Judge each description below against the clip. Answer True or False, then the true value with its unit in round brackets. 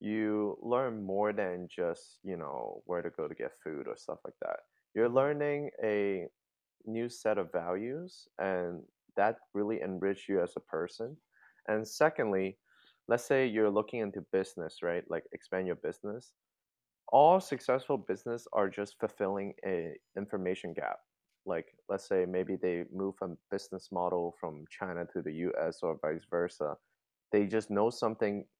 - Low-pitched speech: True (105 Hz)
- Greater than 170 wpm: False (155 wpm)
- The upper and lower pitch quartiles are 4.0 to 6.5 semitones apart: True (4.9 semitones)